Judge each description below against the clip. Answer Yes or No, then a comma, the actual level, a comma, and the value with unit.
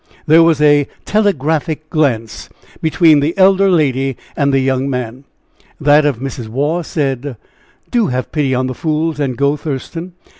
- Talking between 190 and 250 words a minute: No, average, 155 wpm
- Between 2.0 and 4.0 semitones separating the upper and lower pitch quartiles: Yes, average, 3.3 semitones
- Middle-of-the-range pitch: Yes, medium, 145 Hz